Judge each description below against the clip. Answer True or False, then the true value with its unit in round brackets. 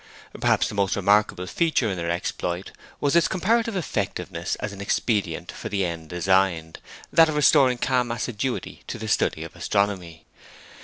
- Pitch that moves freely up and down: True (6.1 semitones)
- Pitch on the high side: False (100 Hz)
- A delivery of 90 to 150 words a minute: False (160 wpm)